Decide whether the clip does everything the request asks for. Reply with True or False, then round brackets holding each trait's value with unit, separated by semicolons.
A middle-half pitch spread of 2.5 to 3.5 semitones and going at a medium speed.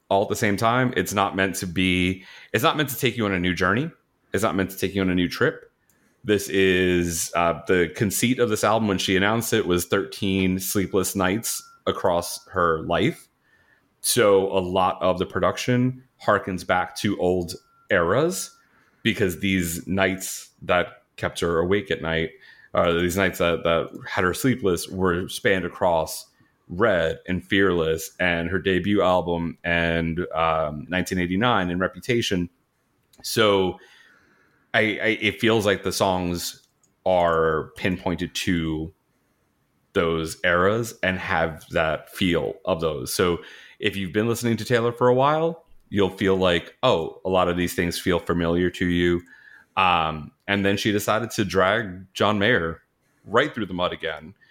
True (2.8 semitones; 165 wpm)